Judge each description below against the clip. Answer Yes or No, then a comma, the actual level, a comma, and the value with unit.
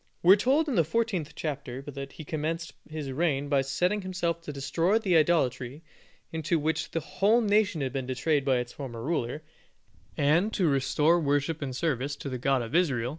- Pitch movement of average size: Yes, average, 4.1 semitones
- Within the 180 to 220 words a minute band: Yes, average, 195 wpm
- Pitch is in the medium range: Yes, medium, 150 Hz